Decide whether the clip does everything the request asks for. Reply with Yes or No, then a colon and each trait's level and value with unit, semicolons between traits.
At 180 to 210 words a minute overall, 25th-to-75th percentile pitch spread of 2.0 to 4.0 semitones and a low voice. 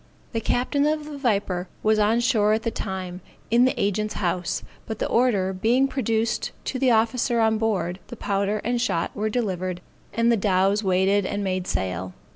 No: average, 185 wpm; average, 3.7 semitones; high, 215 Hz